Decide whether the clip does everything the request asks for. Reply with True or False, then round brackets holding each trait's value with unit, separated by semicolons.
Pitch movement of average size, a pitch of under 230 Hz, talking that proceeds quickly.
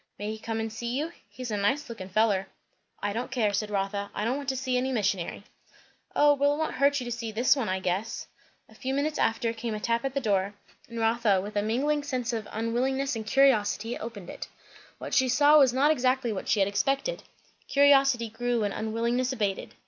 False (4.0 semitones; 235 Hz; 215 wpm)